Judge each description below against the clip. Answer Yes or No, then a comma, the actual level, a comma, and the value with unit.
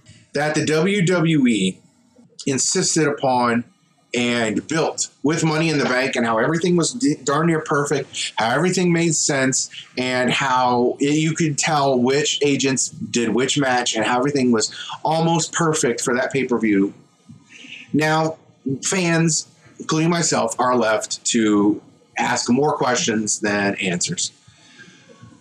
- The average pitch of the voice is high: No, medium, 140 Hz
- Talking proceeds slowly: Yes, slow, 130 wpm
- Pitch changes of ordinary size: Yes, average, 4.6 semitones